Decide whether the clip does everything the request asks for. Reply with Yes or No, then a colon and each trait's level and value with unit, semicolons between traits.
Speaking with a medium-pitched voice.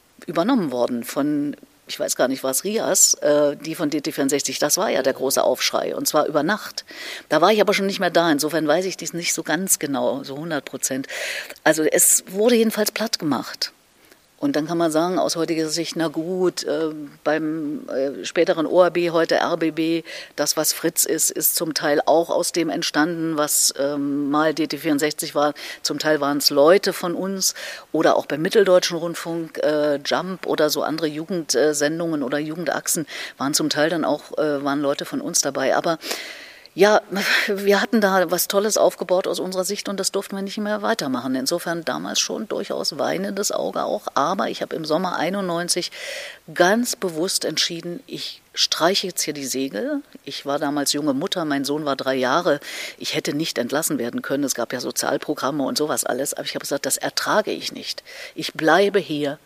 Yes: medium, 165 Hz